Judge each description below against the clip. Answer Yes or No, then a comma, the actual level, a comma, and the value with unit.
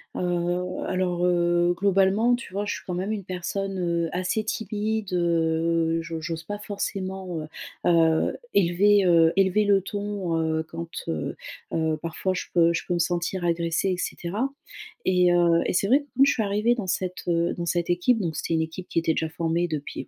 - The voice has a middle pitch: Yes, medium, 175 Hz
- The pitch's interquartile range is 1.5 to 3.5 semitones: Yes, average, 2.8 semitones